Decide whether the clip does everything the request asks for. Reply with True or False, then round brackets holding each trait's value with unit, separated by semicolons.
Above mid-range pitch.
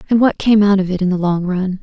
True (195 Hz)